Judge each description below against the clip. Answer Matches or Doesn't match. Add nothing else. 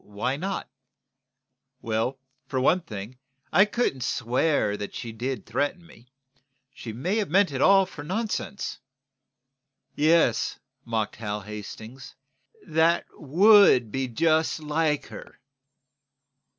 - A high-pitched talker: Doesn't match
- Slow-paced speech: Matches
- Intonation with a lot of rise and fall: Matches